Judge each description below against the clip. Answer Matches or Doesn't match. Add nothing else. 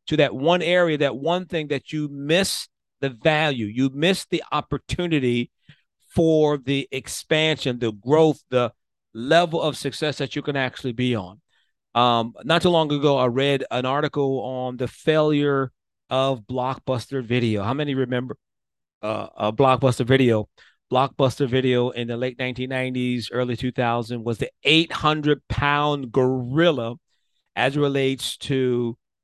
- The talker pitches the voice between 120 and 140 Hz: Matches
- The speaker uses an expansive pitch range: Doesn't match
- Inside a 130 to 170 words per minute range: Matches